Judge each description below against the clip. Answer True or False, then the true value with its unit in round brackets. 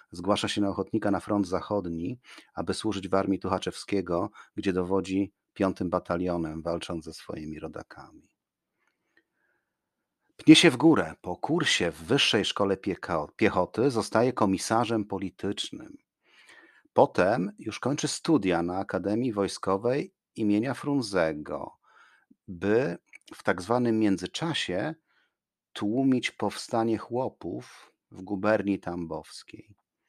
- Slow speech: True (105 wpm)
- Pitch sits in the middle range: False (100 Hz)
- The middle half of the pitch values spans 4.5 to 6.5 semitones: False (3.3 semitones)